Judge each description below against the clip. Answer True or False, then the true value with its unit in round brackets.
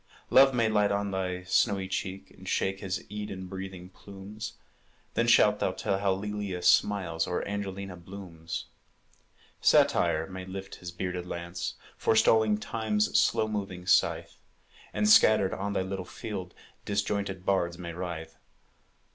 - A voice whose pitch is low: True (95 Hz)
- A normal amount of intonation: False (2.1 semitones)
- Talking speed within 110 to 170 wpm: True (140 wpm)